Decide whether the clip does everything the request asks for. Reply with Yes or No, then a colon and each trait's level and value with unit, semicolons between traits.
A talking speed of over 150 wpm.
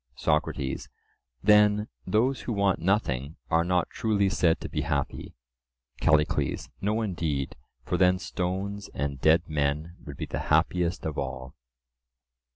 No: slow, 135 wpm